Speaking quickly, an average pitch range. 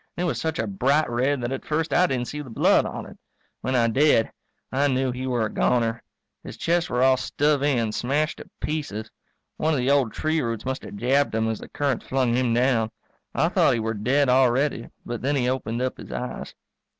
Yes: fast, 225 wpm; average, 3.4 semitones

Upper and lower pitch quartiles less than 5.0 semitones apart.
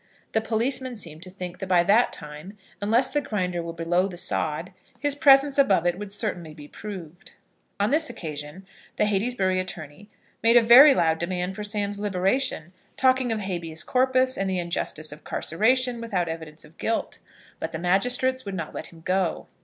No: wide, 5.6 semitones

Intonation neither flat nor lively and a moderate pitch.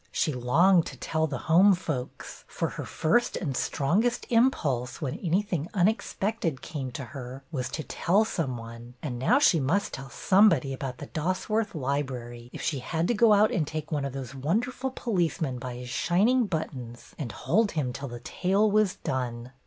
No: wide, 7.1 semitones; medium, 155 Hz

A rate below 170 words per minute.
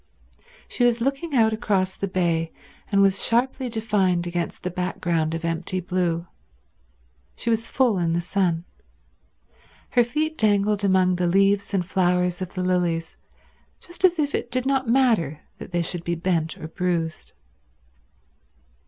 Yes: average, 155 wpm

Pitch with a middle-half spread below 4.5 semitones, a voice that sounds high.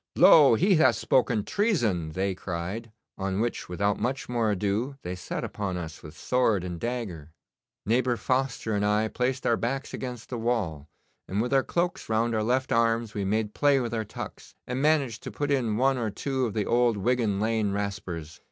No: average, 4.1 semitones; low, 115 Hz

